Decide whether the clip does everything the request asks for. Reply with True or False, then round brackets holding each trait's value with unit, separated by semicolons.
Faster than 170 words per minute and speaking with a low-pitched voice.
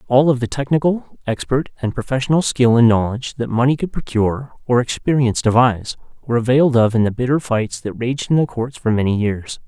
True (200 wpm; 125 Hz)